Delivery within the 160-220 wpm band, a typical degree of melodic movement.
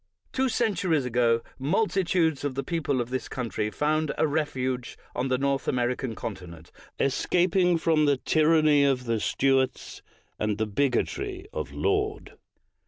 No: average, 150 wpm; average, 4.7 semitones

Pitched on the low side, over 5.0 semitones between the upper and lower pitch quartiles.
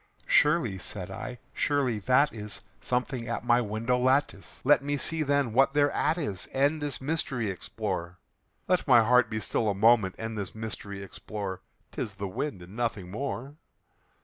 Yes: low, 120 Hz; wide, 5.4 semitones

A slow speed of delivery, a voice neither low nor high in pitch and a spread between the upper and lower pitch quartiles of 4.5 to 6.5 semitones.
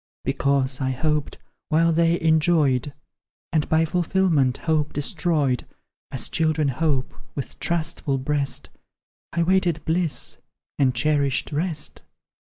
No: slow, 110 wpm; medium, 155 Hz; average, 3.0 semitones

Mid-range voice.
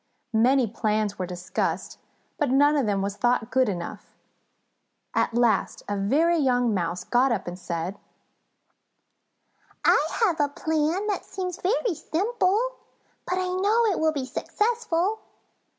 No: very high, 275 Hz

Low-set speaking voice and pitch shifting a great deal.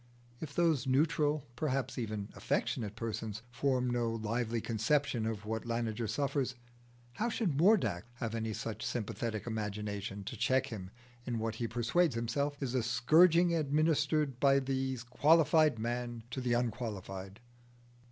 No: low, 120 Hz; average, 4.3 semitones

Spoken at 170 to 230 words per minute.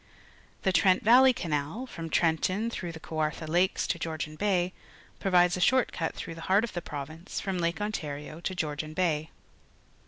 Yes: average, 175 wpm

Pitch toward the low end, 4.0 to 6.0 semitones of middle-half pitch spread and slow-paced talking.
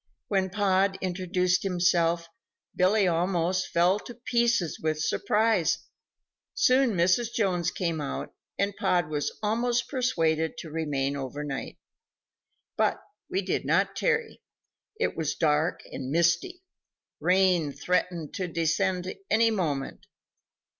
No: medium, 180 Hz; average, 4.3 semitones; slow, 120 wpm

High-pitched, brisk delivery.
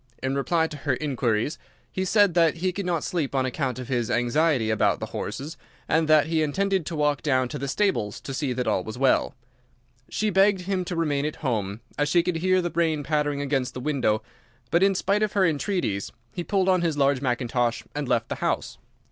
No: medium, 150 Hz; fast, 215 wpm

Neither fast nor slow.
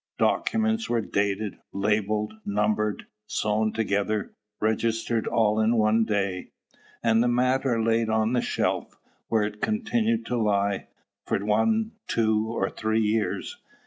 No: slow, 130 wpm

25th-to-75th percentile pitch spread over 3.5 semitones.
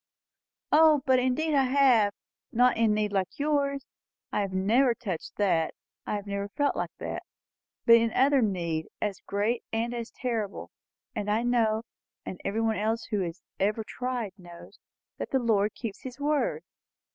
Yes: average, 4.0 semitones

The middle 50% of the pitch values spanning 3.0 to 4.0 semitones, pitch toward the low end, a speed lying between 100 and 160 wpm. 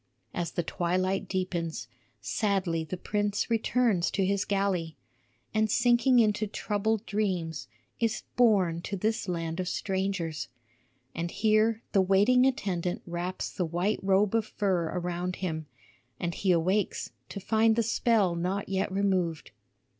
No: average, 3.5 semitones; high, 190 Hz; average, 140 wpm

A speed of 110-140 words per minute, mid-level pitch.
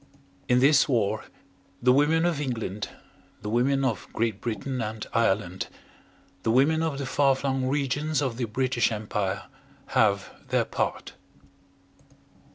No: slow, 135 wpm; low, 125 Hz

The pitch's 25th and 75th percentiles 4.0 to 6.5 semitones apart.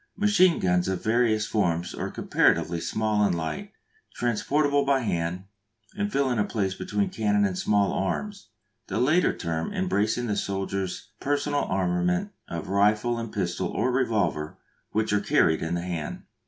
Yes: wide, 5.4 semitones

